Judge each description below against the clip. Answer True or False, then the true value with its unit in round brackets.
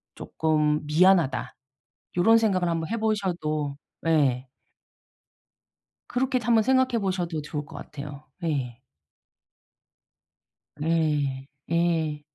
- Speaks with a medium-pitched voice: True (165 Hz)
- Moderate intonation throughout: True (4.4 semitones)